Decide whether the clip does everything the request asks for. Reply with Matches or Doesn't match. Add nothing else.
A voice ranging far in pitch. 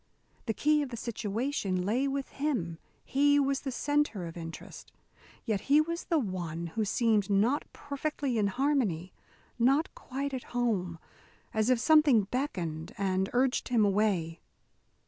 Matches